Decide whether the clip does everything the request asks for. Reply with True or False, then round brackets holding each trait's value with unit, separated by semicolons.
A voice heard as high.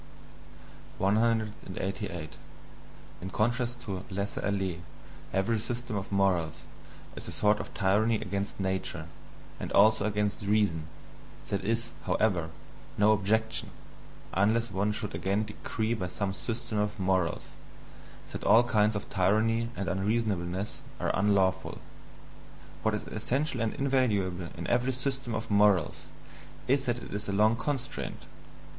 False (105 Hz)